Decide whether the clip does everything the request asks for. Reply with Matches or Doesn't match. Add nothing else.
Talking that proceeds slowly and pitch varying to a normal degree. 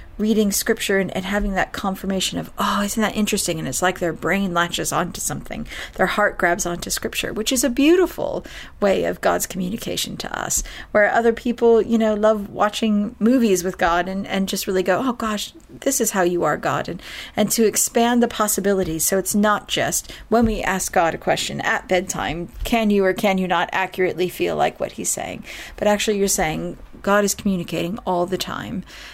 Doesn't match